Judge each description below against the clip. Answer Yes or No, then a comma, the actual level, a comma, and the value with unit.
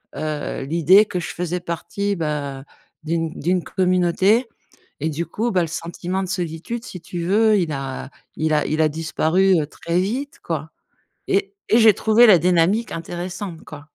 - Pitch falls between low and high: Yes, medium, 175 Hz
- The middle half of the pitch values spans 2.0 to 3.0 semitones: No, average, 3.5 semitones